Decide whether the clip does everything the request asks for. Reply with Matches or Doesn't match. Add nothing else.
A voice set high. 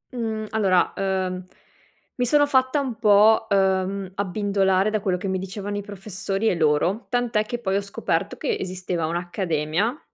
Matches